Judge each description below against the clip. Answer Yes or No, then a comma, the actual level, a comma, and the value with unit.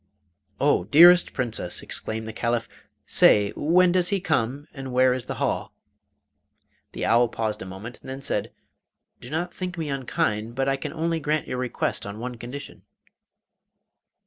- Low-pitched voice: Yes, low, 130 Hz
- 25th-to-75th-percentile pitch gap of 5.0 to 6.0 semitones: Yes, wide, 5.4 semitones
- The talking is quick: No, average, 165 wpm